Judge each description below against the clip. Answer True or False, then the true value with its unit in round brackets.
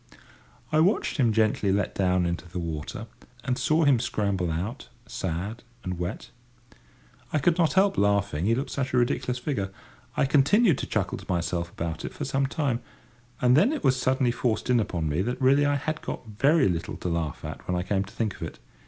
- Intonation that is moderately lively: False (7.1 semitones)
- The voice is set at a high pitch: False (115 Hz)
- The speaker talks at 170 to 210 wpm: True (205 wpm)